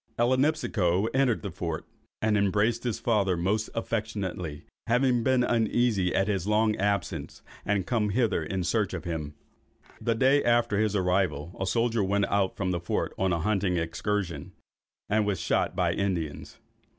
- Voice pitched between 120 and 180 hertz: No, low, 100 Hz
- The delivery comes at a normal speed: Yes, average, 160 wpm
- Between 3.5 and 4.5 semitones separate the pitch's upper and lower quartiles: Yes, average, 4.0 semitones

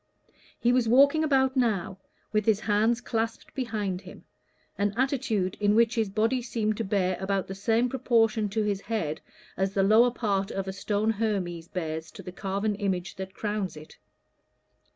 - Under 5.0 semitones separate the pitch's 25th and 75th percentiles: Yes, average, 3.0 semitones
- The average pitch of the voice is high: Yes, high, 210 Hz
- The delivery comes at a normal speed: Yes, average, 175 wpm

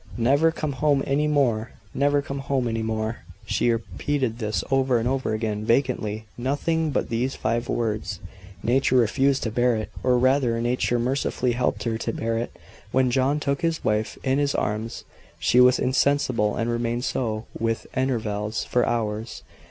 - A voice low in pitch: Yes, low, 120 Hz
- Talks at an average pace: Yes, average, 165 wpm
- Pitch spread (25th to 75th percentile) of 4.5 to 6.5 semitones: No, average, 3.2 semitones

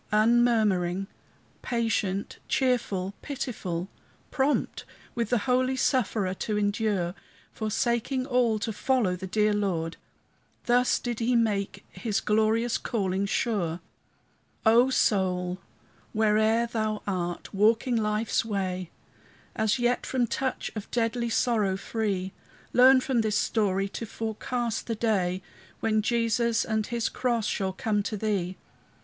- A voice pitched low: No, high, 220 Hz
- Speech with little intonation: No, average, 3.2 semitones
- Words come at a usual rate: No, slow, 120 wpm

